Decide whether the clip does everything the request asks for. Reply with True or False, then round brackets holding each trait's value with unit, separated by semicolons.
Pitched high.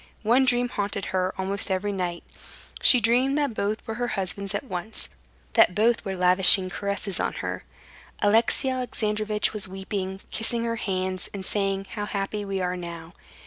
True (200 Hz)